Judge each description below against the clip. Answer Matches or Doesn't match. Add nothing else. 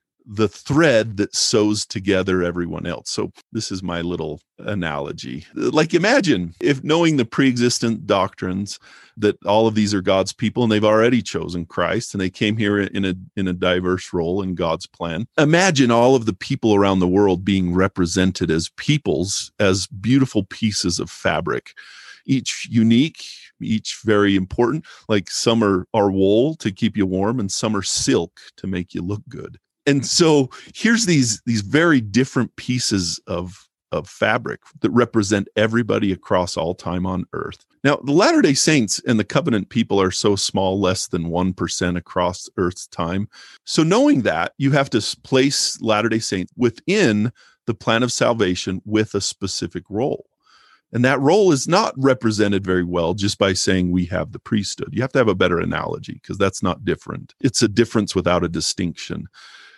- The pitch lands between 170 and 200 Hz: Doesn't match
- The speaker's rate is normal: Matches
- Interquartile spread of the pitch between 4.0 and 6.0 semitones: Matches